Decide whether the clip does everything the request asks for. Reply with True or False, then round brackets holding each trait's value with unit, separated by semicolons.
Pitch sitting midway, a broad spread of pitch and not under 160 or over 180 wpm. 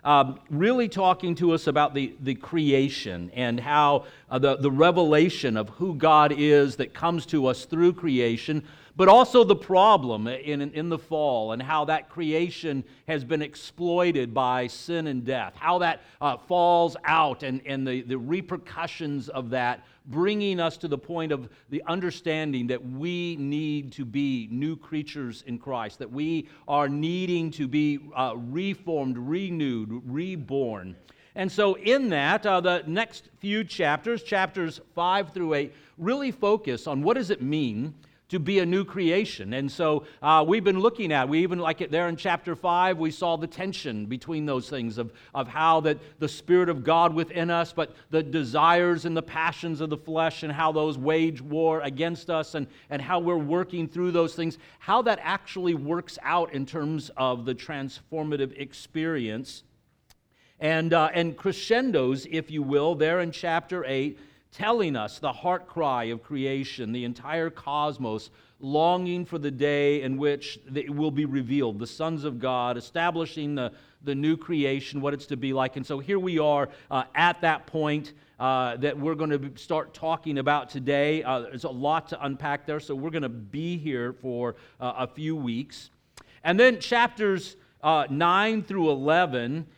False (155 Hz; 3.7 semitones; 175 wpm)